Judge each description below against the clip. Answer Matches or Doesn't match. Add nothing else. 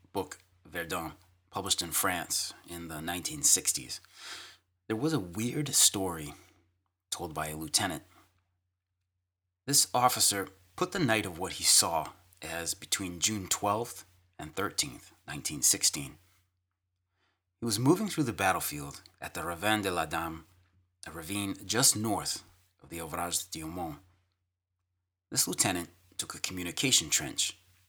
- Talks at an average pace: Doesn't match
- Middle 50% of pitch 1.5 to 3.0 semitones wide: Matches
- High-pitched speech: Doesn't match